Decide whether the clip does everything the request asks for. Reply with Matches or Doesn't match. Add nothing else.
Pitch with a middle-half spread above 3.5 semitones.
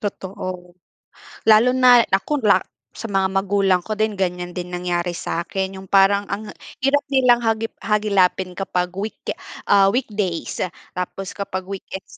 Doesn't match